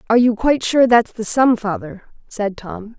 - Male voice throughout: No, female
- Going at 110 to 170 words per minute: No, average, 200 wpm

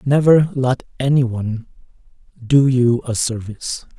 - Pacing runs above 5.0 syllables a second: No, 4.6 syllables/s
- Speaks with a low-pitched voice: Yes, low, 125 Hz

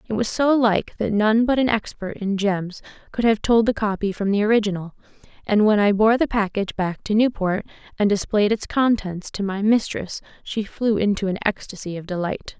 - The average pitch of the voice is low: No, high, 210 Hz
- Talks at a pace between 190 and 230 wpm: Yes, average, 200 wpm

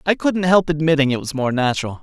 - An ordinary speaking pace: No, fast, 235 wpm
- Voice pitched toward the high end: No, medium, 150 Hz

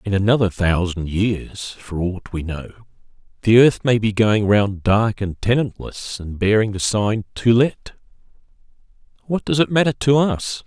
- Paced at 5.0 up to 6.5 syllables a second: No, 4.2 syllables/s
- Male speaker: Yes, male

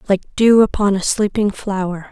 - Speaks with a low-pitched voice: No, high, 200 Hz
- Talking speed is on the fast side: No, average, 170 wpm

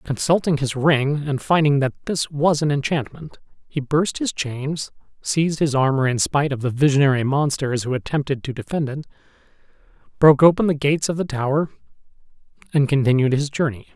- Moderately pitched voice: Yes, medium, 145 Hz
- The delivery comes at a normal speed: Yes, average, 170 wpm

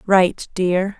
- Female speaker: Yes, female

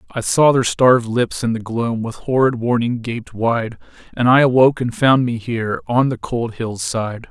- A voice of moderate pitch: No, low, 120 Hz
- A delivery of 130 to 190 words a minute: No, fast, 205 wpm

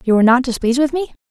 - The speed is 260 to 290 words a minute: Yes, fast, 275 wpm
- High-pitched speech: Yes, very high, 260 Hz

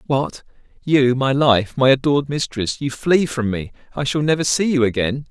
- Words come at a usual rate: Yes, average, 190 wpm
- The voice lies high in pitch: No, low, 135 Hz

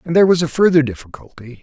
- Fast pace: Yes, fast, 220 wpm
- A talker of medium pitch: Yes, medium, 145 Hz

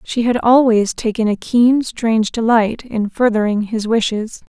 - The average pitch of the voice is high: Yes, high, 225 Hz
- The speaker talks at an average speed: Yes, average, 160 wpm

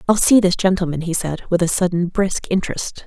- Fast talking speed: Yes, fast, 215 wpm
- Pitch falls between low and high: Yes, medium, 180 Hz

